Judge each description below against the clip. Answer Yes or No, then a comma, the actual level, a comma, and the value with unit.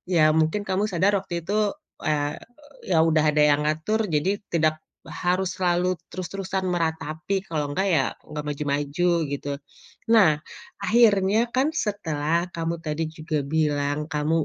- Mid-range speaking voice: Yes, medium, 165 Hz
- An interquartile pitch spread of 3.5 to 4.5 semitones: Yes, average, 4.0 semitones